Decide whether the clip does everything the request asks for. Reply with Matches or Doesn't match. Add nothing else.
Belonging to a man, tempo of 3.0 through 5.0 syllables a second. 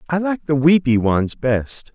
Matches